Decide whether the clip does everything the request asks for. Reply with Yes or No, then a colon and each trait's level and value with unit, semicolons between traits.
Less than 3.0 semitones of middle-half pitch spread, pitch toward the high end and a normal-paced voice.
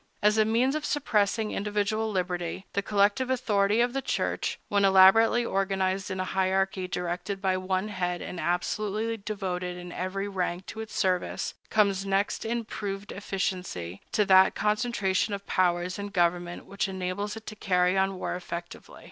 Yes: narrow, 2.4 semitones; high, 195 Hz; average, 165 wpm